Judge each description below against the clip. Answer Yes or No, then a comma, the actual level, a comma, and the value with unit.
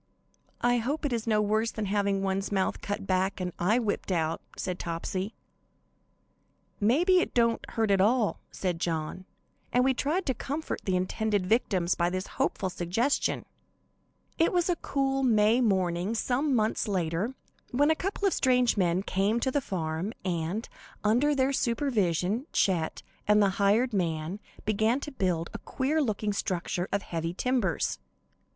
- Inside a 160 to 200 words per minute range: Yes, average, 165 wpm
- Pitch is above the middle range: Yes, high, 210 Hz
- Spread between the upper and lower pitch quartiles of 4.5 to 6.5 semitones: Yes, average, 5.3 semitones